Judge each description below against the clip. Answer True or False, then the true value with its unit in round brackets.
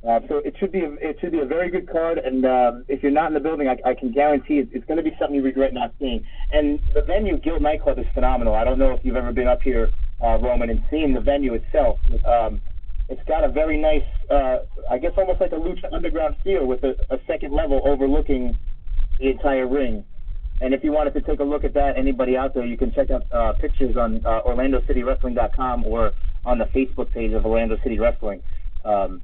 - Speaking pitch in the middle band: False (130 Hz)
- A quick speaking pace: True (235 wpm)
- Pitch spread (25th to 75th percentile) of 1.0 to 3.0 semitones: False (3.8 semitones)